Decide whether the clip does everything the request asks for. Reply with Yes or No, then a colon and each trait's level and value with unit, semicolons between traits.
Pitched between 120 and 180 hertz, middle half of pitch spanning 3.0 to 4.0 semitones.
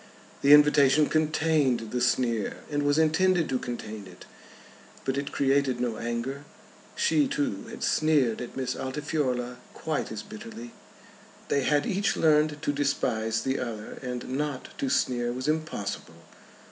Yes: low, 135 Hz; average, 3.7 semitones